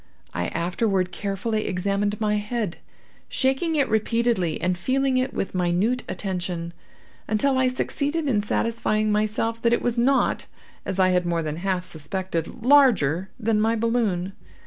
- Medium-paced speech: Yes, average, 145 wpm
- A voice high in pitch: Yes, high, 210 Hz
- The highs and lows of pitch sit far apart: No, average, 4.6 semitones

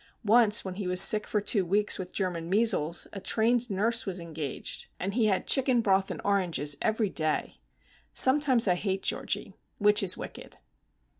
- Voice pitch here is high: Yes, high, 200 Hz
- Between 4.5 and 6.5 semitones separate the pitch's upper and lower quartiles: No, average, 3.4 semitones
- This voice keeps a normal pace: Yes, average, 165 wpm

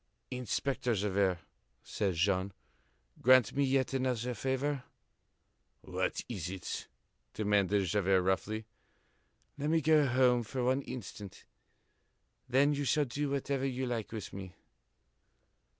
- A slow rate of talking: Yes, slow, 120 wpm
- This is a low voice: Yes, low, 125 Hz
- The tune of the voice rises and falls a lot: No, average, 5.0 semitones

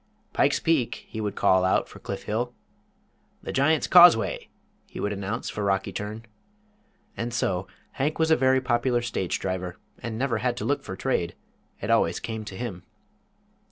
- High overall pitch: No, low, 115 Hz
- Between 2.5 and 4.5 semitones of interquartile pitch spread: No, average, 5.1 semitones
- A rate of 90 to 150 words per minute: No, average, 170 wpm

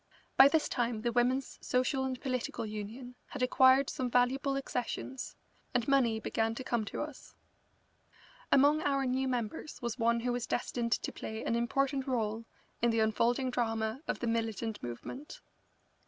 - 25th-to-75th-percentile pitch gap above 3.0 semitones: No, narrow, 2.6 semitones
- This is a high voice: Yes, high, 245 Hz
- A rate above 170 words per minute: No, average, 160 wpm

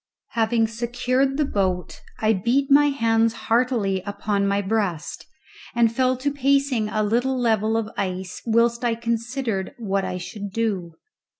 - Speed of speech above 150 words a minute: No, average, 145 wpm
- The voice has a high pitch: Yes, high, 225 Hz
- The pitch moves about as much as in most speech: Yes, average, 3.5 semitones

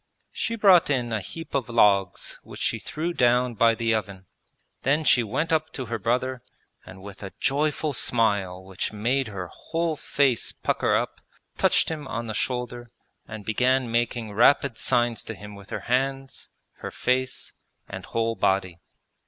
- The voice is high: No, low, 120 Hz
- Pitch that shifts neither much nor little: Yes, average, 4.2 semitones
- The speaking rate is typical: Yes, average, 165 wpm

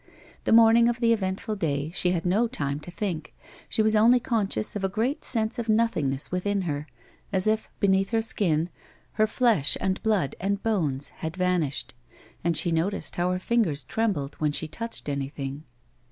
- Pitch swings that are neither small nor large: No, wide, 6.0 semitones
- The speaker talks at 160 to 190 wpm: Yes, average, 180 wpm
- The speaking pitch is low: No, high, 190 Hz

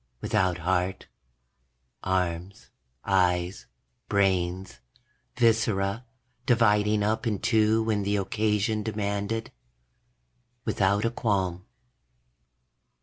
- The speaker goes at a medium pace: No, slow, 80 wpm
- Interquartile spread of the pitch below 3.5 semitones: Yes, narrow, 2.6 semitones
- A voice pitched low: Yes, low, 100 Hz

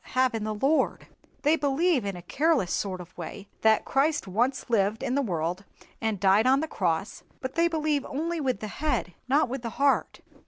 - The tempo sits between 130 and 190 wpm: No, average, 200 wpm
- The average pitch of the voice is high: Yes, very high, 255 Hz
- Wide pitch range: Yes, wide, 6.4 semitones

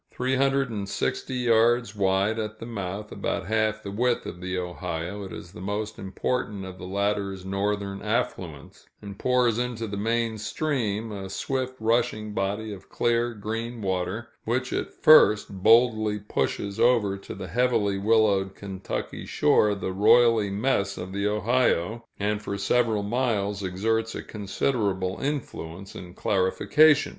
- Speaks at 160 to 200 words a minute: No, average, 150 wpm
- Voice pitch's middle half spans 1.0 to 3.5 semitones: Yes, average, 3.1 semitones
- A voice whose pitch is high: No, low, 105 Hz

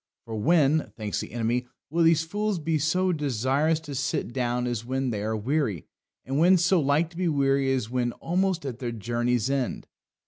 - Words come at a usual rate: Yes, average, 195 wpm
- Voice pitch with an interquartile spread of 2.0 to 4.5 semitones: No, average, 5.2 semitones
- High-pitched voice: No, low, 135 Hz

